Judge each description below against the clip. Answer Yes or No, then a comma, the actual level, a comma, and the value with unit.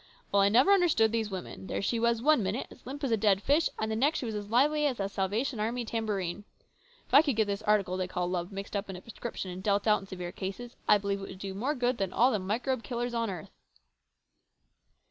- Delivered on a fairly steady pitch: No, average, 3.8 semitones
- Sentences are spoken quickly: Yes, fast, 255 wpm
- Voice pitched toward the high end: Yes, high, 215 Hz